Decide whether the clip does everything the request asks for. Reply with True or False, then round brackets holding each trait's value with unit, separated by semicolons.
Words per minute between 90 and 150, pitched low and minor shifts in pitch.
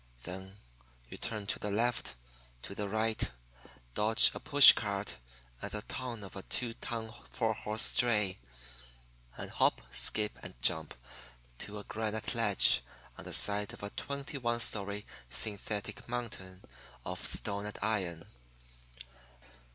True (140 wpm; 105 Hz; 2.2 semitones)